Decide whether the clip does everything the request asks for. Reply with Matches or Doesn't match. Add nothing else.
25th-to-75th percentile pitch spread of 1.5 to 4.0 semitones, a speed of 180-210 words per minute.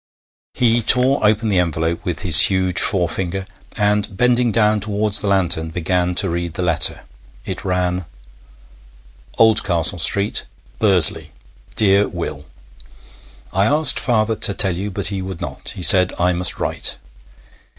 Doesn't match